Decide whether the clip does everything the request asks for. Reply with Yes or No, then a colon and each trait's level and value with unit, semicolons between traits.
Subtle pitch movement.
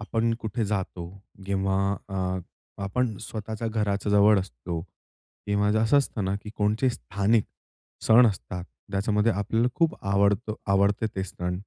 Yes: narrow, 2.3 semitones